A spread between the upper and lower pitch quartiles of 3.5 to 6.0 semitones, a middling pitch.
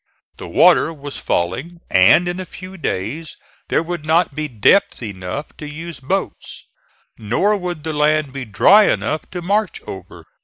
Yes: average, 5.2 semitones; medium, 155 Hz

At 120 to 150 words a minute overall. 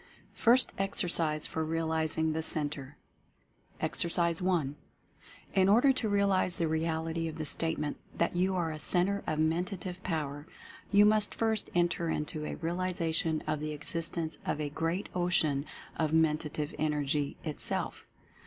Yes: average, 140 wpm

